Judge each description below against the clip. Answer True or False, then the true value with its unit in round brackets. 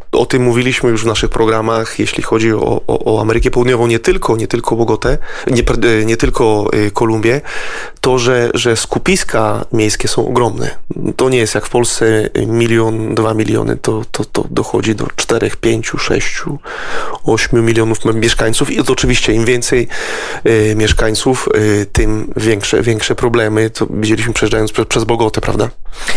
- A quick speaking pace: False (150 wpm)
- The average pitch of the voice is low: True (115 Hz)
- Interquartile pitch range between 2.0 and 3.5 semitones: False (1.6 semitones)